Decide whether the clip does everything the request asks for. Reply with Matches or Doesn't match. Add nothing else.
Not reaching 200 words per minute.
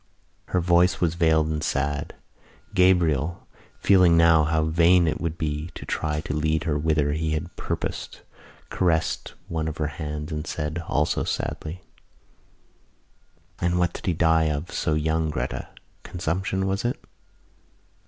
Matches